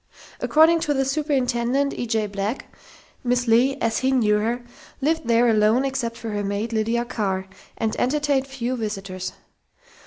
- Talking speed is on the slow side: No, average, 155 wpm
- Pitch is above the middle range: Yes, high, 235 Hz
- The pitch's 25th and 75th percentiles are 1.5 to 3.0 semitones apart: No, average, 3.8 semitones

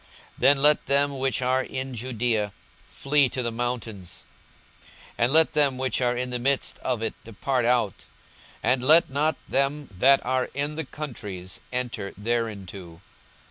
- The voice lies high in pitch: No, low, 125 Hz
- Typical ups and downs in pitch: Yes, average, 3.3 semitones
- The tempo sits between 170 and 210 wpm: No, average, 155 wpm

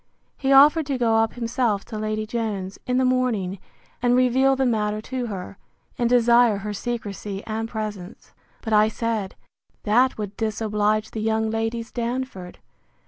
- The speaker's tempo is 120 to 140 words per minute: No, average, 150 wpm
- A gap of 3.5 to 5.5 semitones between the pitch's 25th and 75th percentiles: No, narrow, 2.6 semitones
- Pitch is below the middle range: No, high, 225 Hz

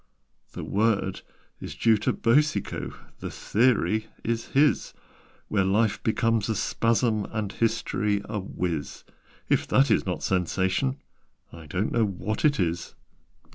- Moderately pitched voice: No, low, 110 Hz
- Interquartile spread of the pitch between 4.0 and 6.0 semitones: No, average, 3.2 semitones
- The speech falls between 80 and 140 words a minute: Yes, slow, 135 wpm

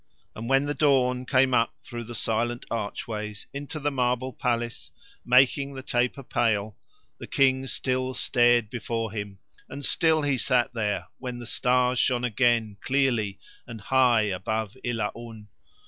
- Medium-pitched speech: No, low, 120 Hz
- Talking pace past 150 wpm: No, average, 145 wpm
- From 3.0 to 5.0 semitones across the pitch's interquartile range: No, narrow, 2.6 semitones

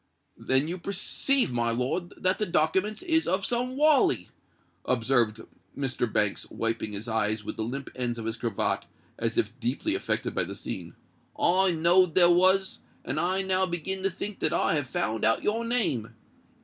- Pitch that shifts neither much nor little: No, wide, 8.4 semitones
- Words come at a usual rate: Yes, average, 175 wpm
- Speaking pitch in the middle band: Yes, medium, 160 Hz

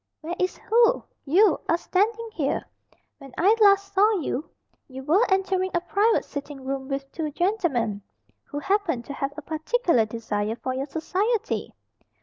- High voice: Yes, very high, 330 Hz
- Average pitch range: No, wide, 6.6 semitones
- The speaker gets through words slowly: No, average, 155 wpm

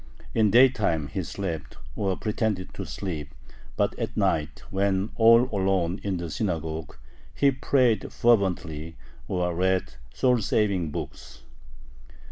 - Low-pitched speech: Yes, very low, 95 Hz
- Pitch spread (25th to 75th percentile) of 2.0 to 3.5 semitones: No, average, 4.7 semitones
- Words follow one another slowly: Yes, slow, 120 wpm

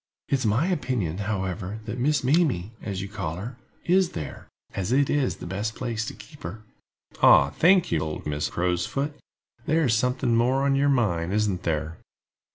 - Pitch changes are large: Yes, wide, 7.0 semitones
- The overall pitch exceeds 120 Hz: No, low, 110 Hz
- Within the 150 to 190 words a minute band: Yes, average, 185 wpm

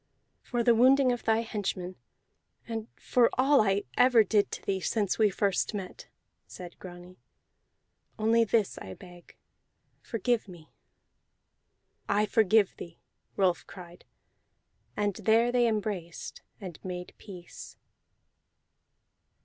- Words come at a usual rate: No, slow, 115 wpm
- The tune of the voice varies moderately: Yes, average, 4.0 semitones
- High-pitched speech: Yes, high, 205 Hz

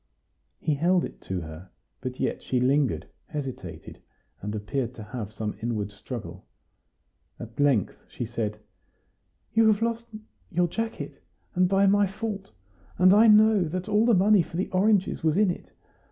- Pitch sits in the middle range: Yes, medium, 165 Hz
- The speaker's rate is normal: Yes, average, 160 wpm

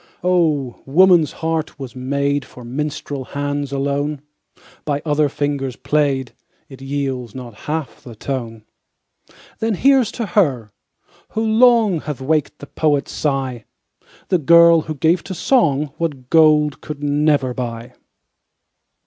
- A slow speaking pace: Yes, slow, 130 wpm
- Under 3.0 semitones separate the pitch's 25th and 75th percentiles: No, average, 3.3 semitones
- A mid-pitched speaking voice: Yes, medium, 145 Hz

